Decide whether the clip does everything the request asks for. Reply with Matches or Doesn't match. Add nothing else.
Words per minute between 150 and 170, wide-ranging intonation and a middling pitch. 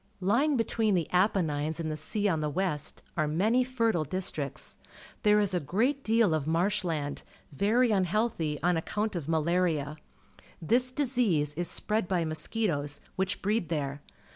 Matches